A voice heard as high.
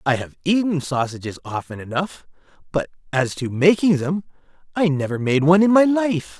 No: medium, 160 Hz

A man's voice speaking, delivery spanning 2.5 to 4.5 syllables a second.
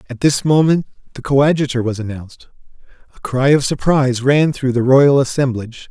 No: male; 5.7 syllables/s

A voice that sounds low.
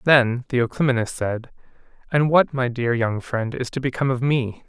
Yes: low, 125 Hz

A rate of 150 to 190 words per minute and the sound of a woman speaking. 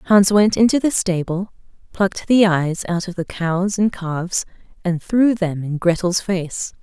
Yes: average, 175 wpm; female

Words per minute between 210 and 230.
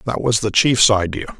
Yes: fast, 215 wpm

